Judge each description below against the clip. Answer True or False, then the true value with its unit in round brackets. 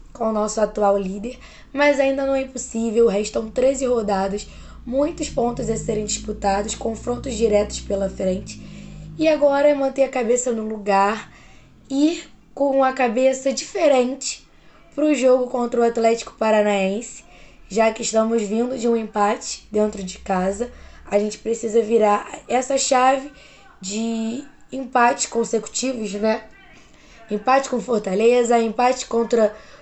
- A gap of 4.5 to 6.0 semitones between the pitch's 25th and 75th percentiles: False (3.6 semitones)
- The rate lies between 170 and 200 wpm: False (135 wpm)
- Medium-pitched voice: False (230 Hz)